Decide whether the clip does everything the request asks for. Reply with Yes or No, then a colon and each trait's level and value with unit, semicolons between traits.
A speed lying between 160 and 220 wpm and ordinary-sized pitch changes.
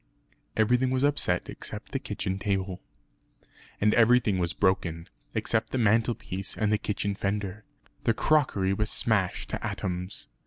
No: average, 140 wpm; average, 3.2 semitones